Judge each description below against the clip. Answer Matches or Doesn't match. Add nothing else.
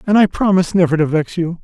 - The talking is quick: Matches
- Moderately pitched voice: Matches